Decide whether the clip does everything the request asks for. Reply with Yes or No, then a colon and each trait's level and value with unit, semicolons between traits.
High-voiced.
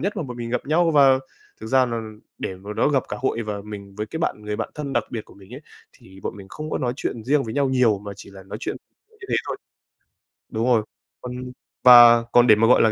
No: low, 120 Hz